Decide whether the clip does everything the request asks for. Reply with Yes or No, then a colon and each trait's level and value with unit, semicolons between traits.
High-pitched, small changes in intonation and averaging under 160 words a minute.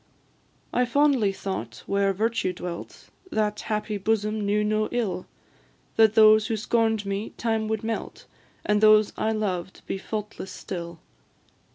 Yes: high, 215 Hz; narrow, 1.9 semitones; average, 140 wpm